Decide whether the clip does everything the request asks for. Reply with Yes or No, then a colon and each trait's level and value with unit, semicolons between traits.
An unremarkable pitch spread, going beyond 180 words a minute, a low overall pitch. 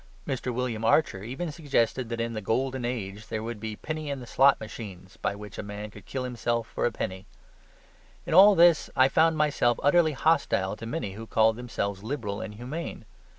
Yes: average, 4.8 semitones; average, 195 wpm; low, 120 Hz